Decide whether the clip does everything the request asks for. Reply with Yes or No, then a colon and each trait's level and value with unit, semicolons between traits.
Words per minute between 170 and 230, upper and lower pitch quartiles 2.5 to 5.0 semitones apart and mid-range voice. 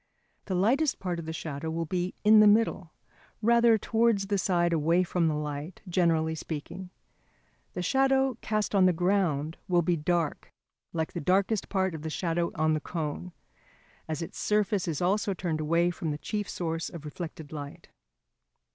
Yes: average, 175 wpm; average, 3.8 semitones; medium, 175 Hz